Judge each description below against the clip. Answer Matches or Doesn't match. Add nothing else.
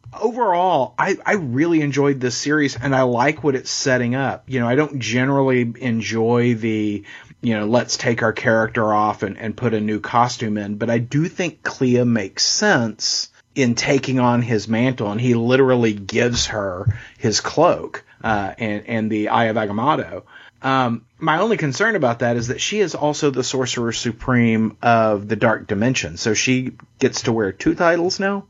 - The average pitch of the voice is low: Matches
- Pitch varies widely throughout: Doesn't match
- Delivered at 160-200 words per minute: Matches